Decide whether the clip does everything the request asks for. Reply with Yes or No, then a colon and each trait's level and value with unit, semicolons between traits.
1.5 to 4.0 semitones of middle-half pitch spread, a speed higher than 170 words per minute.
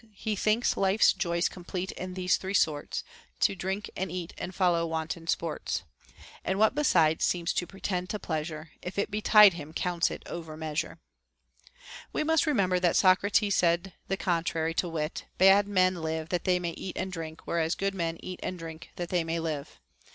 Yes: average, 2.8 semitones; average, 185 wpm